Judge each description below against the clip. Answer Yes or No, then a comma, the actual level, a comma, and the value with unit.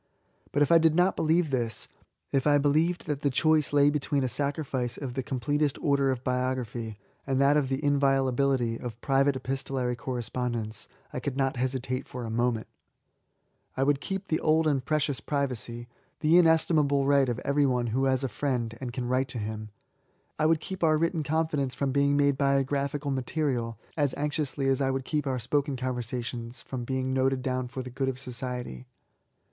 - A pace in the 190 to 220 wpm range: Yes, fast, 205 wpm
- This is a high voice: No, low, 135 Hz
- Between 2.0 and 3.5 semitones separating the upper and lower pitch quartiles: Yes, narrow, 2.5 semitones